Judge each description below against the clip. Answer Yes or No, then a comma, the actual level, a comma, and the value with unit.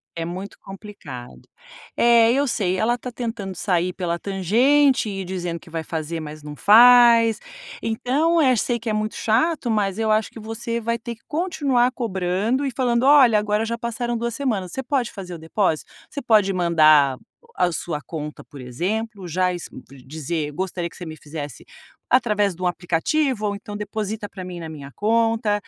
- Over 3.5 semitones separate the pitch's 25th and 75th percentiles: Yes, average, 5.2 semitones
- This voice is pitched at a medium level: No, high, 210 Hz